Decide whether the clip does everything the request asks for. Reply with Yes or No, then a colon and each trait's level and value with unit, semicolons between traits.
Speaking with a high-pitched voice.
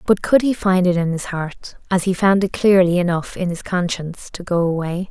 No: medium, 180 Hz